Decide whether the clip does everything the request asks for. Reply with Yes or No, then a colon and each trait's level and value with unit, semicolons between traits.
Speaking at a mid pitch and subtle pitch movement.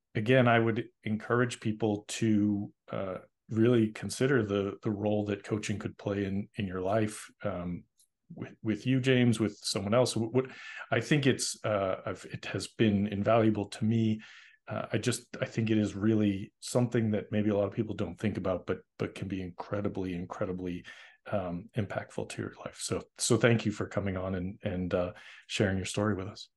No: low, 110 Hz; narrow, 2.3 semitones